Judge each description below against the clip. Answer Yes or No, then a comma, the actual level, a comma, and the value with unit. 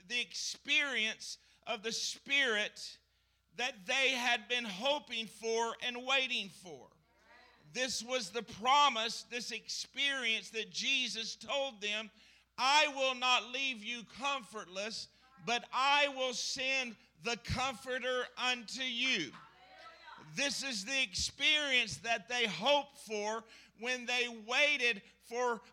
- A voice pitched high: Yes, high, 245 Hz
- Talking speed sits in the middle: No, slow, 115 wpm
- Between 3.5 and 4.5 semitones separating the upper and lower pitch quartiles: No, average, 2.8 semitones